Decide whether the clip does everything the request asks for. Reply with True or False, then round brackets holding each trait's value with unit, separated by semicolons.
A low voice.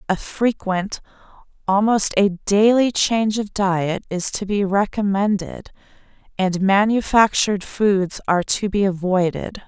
False (200 Hz)